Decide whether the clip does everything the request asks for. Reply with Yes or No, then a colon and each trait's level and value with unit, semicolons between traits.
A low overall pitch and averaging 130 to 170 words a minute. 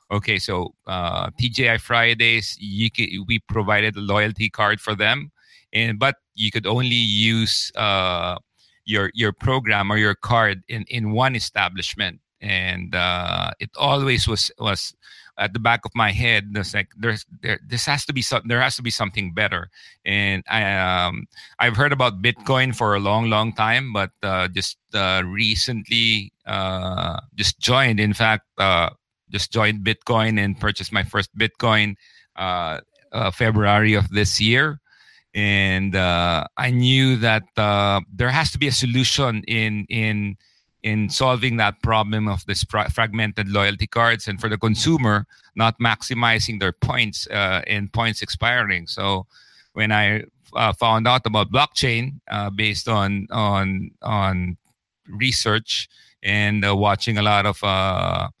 Yes: low, 110 Hz; average, 155 wpm